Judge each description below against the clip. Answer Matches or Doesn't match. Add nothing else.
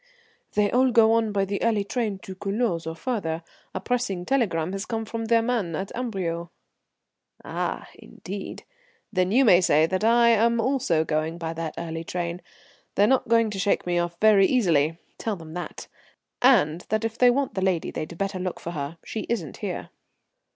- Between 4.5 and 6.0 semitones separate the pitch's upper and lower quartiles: Matches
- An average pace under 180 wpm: Doesn't match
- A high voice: Matches